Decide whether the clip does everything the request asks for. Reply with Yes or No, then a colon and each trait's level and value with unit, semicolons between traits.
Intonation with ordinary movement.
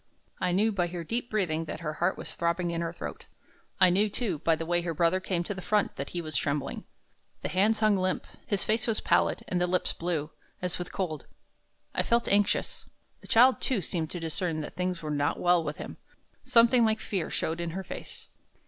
Yes: average, 3.7 semitones